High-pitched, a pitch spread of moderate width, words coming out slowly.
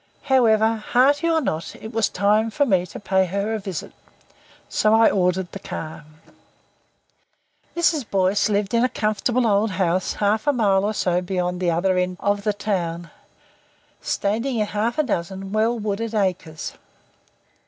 No: high, 205 Hz; average, 3.2 semitones; average, 160 wpm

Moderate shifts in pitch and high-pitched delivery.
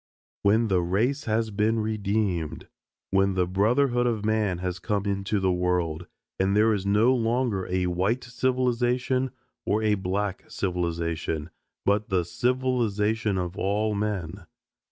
No: average, 3.5 semitones; low, 105 Hz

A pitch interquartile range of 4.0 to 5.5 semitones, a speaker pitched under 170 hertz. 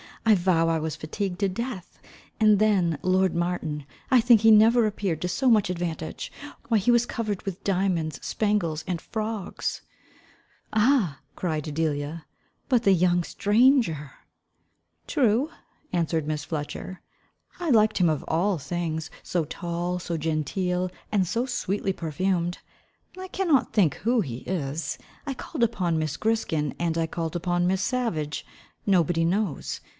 No: average, 4.9 semitones; medium, 180 Hz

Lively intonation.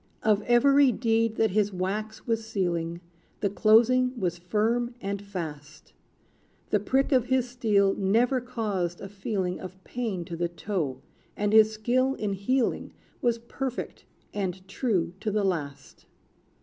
No: average, 4.3 semitones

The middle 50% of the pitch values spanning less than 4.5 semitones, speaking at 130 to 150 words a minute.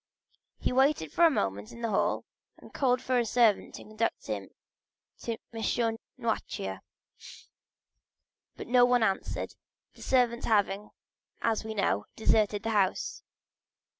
Yes: average, 3.3 semitones; slow, 135 wpm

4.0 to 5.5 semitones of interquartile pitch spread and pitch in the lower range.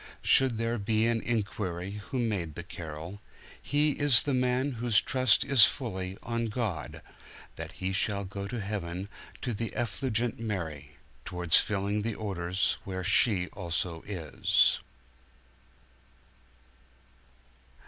Yes: average, 4.4 semitones; low, 105 Hz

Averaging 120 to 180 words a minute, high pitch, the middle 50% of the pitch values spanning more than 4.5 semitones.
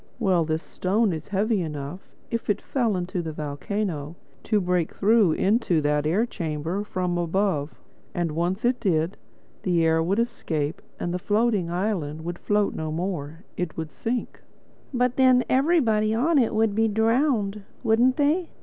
Yes: average, 160 wpm; high, 195 Hz; wide, 5.4 semitones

